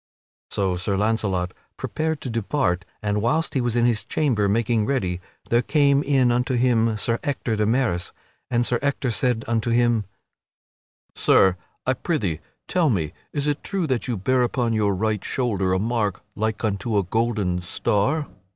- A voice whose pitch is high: No, low, 115 Hz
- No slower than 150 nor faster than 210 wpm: Yes, average, 170 wpm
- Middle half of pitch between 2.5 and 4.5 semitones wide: Yes, average, 3.9 semitones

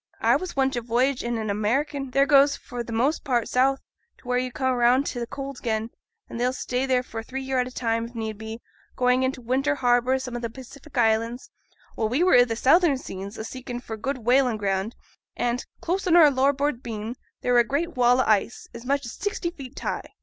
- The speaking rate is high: Yes, fast, 235 wpm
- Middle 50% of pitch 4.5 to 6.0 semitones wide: No, average, 2.7 semitones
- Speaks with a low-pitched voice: No, very high, 250 Hz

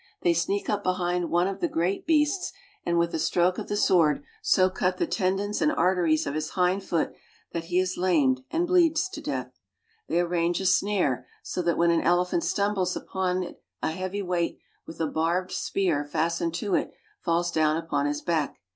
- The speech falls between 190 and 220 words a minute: Yes, average, 200 wpm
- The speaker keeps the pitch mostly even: Yes, narrow, 2.3 semitones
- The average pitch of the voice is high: No, medium, 180 Hz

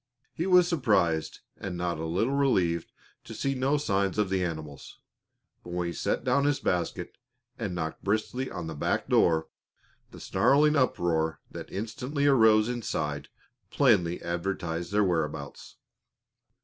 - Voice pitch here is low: Yes, very low, 95 Hz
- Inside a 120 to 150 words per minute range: Yes, average, 145 wpm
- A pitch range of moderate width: No, wide, 7.2 semitones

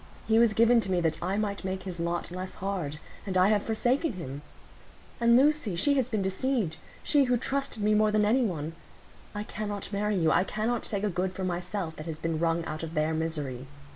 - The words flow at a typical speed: No, fast, 215 wpm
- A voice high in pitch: Yes, high, 195 Hz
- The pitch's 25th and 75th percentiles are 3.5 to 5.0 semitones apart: Yes, average, 4.6 semitones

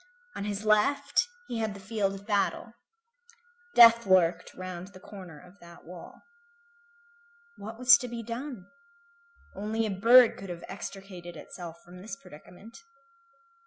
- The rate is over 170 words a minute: No, average, 140 wpm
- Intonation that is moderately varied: Yes, average, 3.8 semitones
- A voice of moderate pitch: No, high, 200 Hz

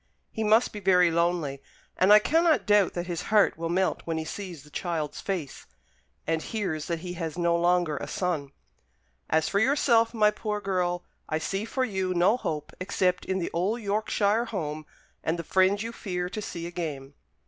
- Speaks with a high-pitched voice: No, medium, 180 Hz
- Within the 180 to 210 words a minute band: Yes, average, 190 wpm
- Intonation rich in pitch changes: No, average, 3.8 semitones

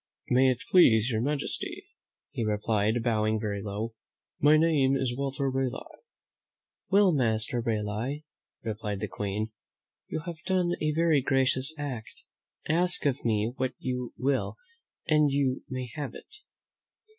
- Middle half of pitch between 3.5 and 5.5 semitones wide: Yes, average, 4.7 semitones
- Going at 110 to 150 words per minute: Yes, slow, 135 wpm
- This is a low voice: Yes, low, 130 Hz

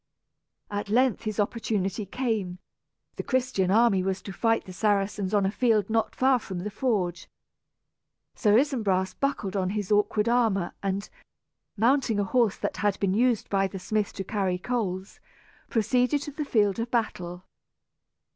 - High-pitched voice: Yes, high, 210 Hz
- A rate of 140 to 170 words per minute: Yes, average, 155 wpm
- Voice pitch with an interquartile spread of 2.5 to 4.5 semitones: Yes, average, 3.5 semitones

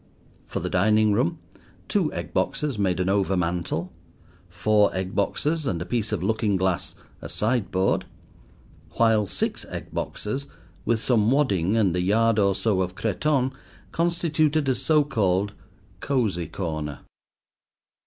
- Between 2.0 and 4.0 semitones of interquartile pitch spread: No, average, 4.9 semitones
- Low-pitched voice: Yes, low, 105 Hz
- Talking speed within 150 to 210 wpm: No, slow, 135 wpm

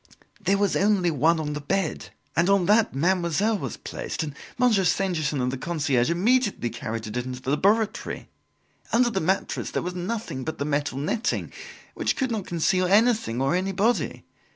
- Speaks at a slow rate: No, average, 175 wpm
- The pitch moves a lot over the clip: Yes, wide, 5.7 semitones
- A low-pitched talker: No, medium, 180 Hz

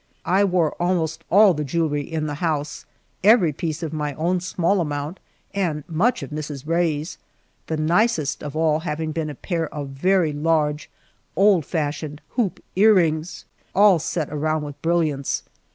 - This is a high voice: No, medium, 160 Hz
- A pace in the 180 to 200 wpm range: No, average, 155 wpm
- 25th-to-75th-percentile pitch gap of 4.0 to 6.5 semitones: No, average, 2.9 semitones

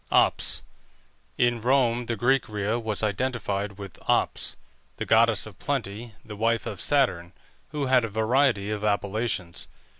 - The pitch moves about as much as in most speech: Yes, average, 3.0 semitones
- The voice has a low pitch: Yes, low, 110 Hz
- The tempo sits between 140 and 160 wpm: Yes, average, 145 wpm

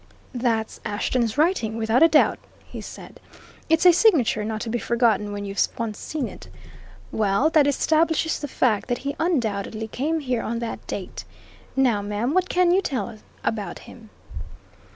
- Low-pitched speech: No, high, 240 Hz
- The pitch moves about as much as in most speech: No, wide, 6.0 semitones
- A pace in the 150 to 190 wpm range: Yes, average, 165 wpm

